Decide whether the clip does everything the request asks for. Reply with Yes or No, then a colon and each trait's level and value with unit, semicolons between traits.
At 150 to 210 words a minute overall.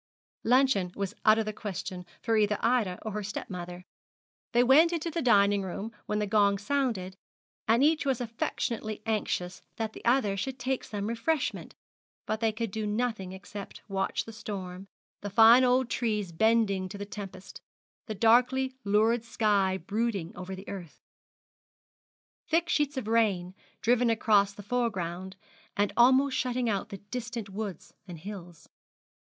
Yes: average, 155 wpm